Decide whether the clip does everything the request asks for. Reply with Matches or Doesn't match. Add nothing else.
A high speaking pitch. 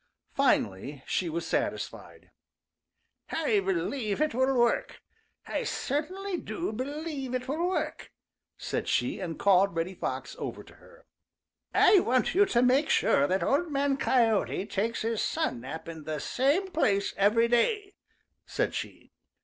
Matches